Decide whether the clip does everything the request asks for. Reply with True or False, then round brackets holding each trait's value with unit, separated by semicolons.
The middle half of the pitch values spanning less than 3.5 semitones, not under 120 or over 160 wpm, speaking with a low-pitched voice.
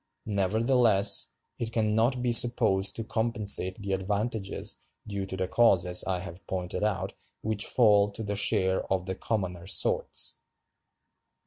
True (2.9 semitones; 140 wpm; 100 Hz)